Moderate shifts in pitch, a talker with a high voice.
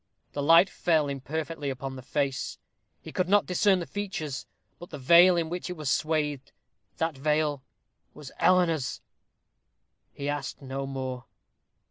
No: average, 3.9 semitones; medium, 150 Hz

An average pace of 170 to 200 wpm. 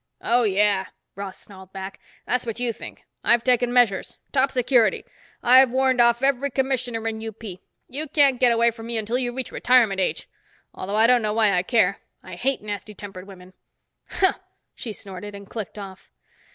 Yes: average, 180 wpm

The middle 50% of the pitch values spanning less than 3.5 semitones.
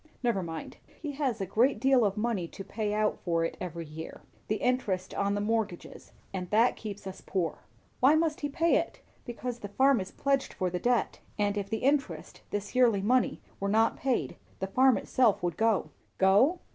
No: average, 4.8 semitones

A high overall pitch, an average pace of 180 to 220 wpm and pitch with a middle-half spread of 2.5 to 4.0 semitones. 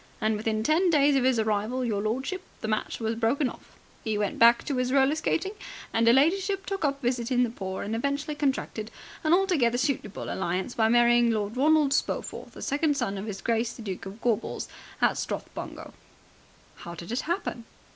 No: high, 240 Hz; average, 190 wpm; average, 4.6 semitones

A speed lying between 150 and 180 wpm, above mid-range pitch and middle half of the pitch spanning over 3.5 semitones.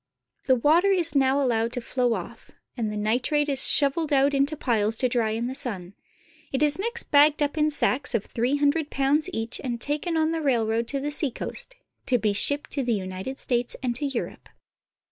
No: average, 200 wpm; very high, 270 Hz; average, 3.9 semitones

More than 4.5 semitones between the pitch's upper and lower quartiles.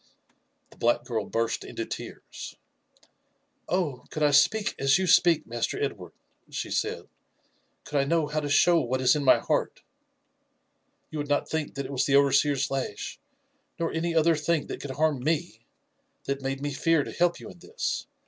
No: average, 3.2 semitones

